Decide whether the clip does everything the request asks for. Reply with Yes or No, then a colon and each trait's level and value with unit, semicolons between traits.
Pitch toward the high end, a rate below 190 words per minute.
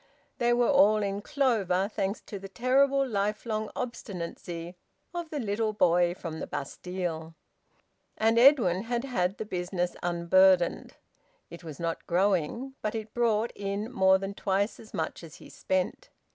Yes: high, 200 Hz; average, 150 wpm